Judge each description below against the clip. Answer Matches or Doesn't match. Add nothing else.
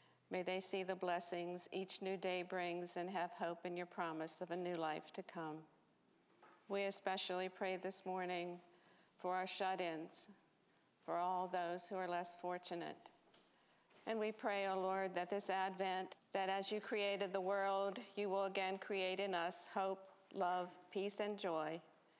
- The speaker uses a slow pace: Doesn't match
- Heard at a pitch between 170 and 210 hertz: Matches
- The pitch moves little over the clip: Matches